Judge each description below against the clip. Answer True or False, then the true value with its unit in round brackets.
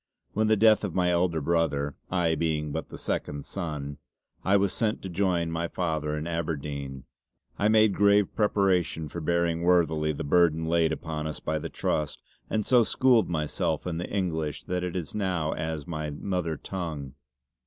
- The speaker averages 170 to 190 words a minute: True (180 wpm)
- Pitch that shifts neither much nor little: True (3.2 semitones)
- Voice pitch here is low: True (85 Hz)